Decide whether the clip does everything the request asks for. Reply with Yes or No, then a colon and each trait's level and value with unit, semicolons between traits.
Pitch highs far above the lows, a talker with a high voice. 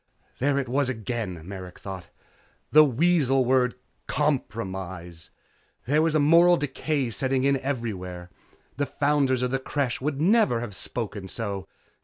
No: wide, 6.0 semitones; low, 130 Hz